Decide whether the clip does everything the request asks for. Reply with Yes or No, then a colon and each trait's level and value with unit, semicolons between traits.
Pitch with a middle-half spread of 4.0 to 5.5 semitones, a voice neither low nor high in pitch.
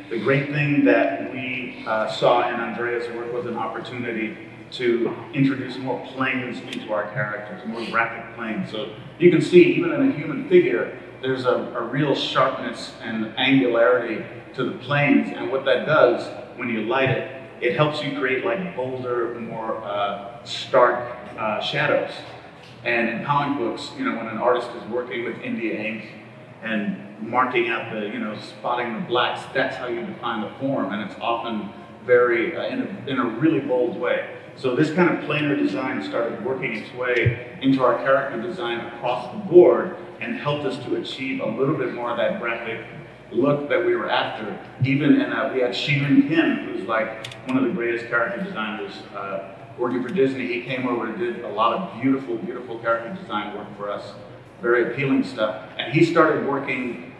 No: average, 4.6 semitones; low, 125 Hz